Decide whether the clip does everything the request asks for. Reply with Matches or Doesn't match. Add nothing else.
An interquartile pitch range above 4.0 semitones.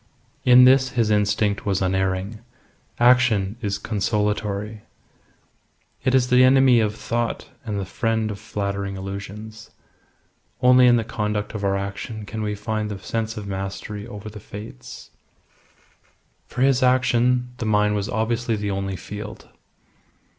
Doesn't match